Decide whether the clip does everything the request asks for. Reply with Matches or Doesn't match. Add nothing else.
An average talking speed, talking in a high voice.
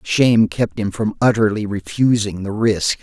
Doesn't match